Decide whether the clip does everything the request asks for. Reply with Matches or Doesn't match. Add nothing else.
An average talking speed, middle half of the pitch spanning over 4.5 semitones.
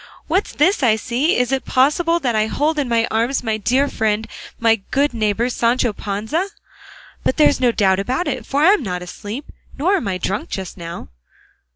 Matches